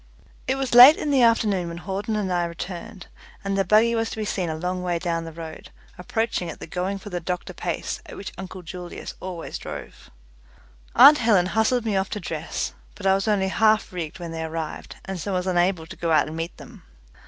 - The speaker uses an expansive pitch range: No, average, 3.8 semitones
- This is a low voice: No, medium, 185 Hz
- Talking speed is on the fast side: Yes, fast, 220 wpm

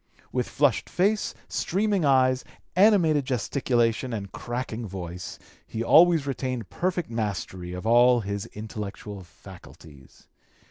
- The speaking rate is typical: No, slow, 110 wpm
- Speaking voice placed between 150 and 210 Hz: No, low, 120 Hz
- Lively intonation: Yes, wide, 6.0 semitones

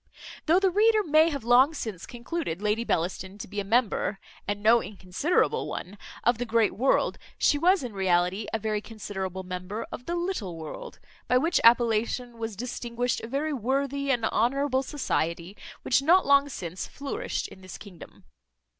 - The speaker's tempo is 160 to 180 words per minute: Yes, average, 170 wpm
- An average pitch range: No, wide, 5.7 semitones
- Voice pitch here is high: Yes, high, 235 Hz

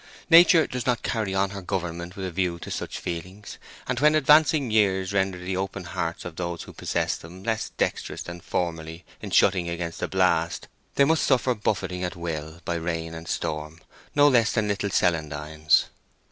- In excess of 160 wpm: Yes, average, 185 wpm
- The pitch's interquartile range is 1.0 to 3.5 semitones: No, average, 4.0 semitones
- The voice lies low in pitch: Yes, very low, 90 Hz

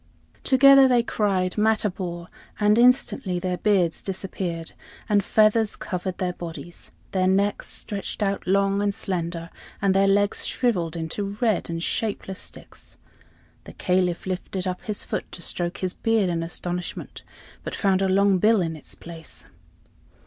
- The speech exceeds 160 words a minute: No, average, 150 wpm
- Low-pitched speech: No, high, 190 Hz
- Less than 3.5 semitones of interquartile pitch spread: Yes, average, 2.7 semitones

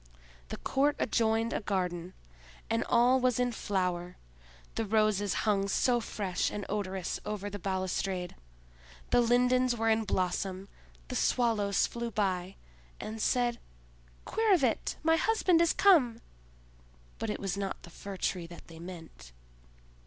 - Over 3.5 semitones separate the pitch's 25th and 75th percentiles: Yes, average, 4.4 semitones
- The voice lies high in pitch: Yes, high, 210 Hz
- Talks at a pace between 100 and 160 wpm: Yes, average, 140 wpm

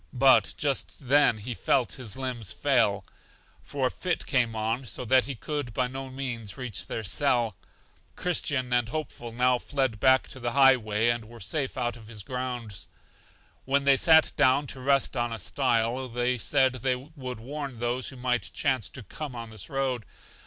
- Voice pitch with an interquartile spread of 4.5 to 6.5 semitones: No, average, 2.7 semitones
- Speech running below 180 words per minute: No, average, 190 wpm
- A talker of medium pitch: No, low, 125 Hz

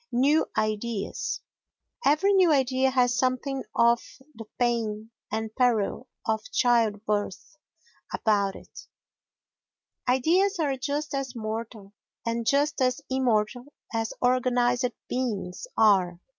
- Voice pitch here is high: Yes, high, 245 Hz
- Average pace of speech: No, slow, 105 wpm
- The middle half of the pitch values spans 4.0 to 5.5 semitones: No, average, 3.4 semitones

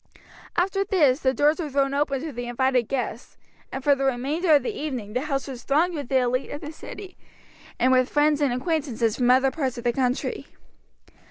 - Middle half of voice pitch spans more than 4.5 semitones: No, average, 3.0 semitones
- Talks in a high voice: Yes, very high, 270 Hz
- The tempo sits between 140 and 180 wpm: No, fast, 205 wpm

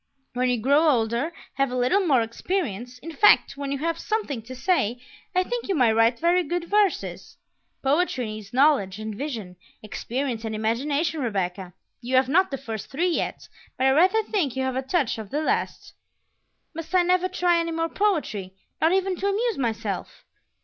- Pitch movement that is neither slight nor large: No, wide, 7.0 semitones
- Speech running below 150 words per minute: No, average, 185 wpm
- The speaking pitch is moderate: No, very high, 275 Hz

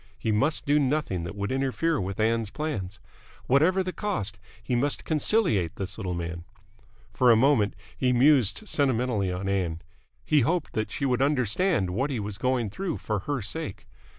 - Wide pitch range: Yes, wide, 6.6 semitones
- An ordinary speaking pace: Yes, average, 170 wpm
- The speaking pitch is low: Yes, low, 125 Hz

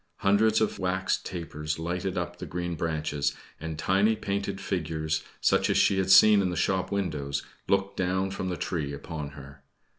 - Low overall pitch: Yes, very low, 90 Hz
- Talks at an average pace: Yes, average, 175 wpm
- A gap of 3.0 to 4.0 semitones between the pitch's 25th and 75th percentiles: Yes, average, 3.7 semitones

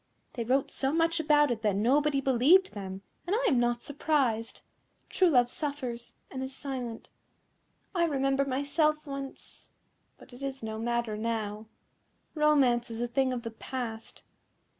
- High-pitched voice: Yes, very high, 260 Hz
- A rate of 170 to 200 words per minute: No, average, 155 wpm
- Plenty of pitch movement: No, average, 3.7 semitones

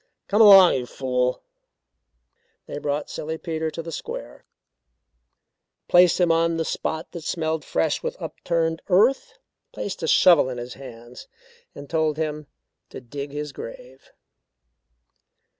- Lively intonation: No, average, 3.8 semitones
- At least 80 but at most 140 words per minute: Yes, slow, 135 wpm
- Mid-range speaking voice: Yes, medium, 160 Hz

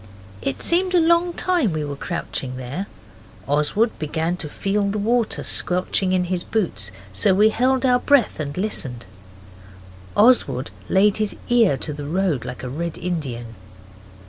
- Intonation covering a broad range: Yes, wide, 7.3 semitones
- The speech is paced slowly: No, average, 155 wpm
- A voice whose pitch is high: No, medium, 180 Hz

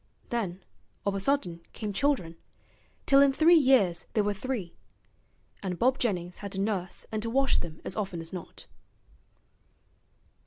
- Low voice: No, high, 205 Hz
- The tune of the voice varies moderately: No, wide, 6.3 semitones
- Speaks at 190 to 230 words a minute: No, average, 155 wpm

